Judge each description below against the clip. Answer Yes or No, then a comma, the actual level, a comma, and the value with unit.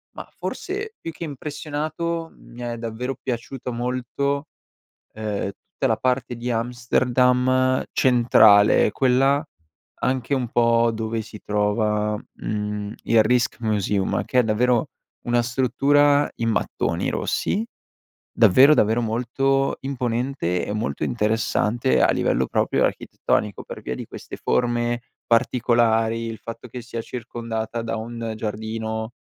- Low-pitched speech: Yes, low, 120 Hz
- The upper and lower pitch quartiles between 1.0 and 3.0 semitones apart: Yes, narrow, 2.6 semitones